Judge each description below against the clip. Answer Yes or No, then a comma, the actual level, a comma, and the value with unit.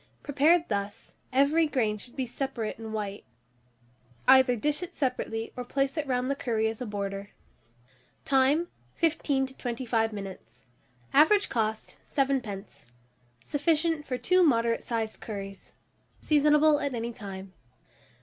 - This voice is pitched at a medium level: No, very high, 250 Hz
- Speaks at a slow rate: Yes, slow, 130 wpm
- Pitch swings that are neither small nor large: Yes, average, 4.9 semitones